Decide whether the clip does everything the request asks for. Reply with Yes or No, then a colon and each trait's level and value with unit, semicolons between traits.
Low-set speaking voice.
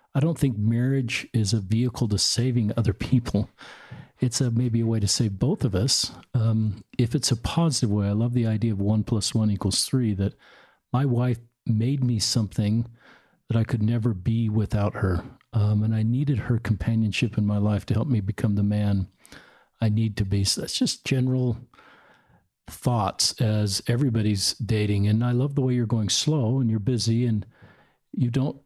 Yes: low, 115 Hz